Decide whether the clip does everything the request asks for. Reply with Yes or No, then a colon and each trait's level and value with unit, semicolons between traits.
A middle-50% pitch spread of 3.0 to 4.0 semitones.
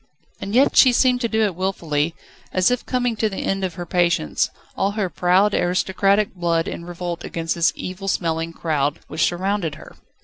Yes: average, 3.4 semitones